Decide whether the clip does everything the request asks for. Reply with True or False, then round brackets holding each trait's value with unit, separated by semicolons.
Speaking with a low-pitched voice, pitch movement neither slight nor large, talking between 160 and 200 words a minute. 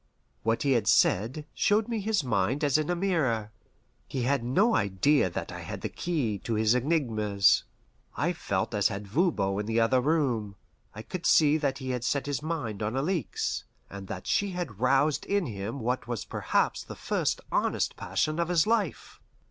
False (130 Hz; 6.4 semitones; 190 wpm)